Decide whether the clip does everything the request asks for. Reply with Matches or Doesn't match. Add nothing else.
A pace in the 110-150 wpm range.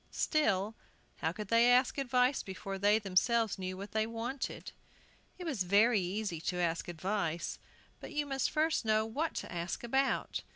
Doesn't match